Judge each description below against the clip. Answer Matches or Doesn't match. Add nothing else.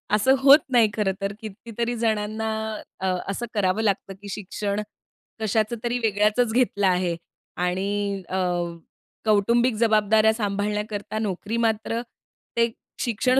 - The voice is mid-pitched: Doesn't match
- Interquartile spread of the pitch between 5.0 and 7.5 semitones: Doesn't match